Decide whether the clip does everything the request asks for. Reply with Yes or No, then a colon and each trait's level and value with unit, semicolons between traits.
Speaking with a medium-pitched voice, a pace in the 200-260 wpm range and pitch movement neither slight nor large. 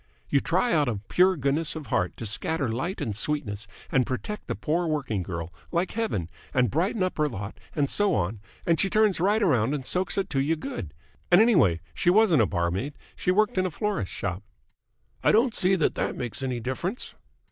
No: medium, 150 Hz; fast, 205 wpm; wide, 8.6 semitones